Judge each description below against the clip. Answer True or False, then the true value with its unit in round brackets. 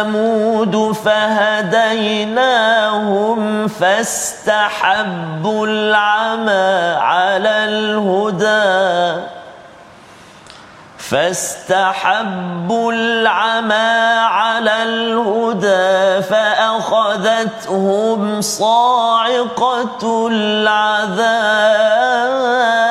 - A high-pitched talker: True (215 Hz)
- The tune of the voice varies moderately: False (1.4 semitones)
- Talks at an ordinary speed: False (30 wpm)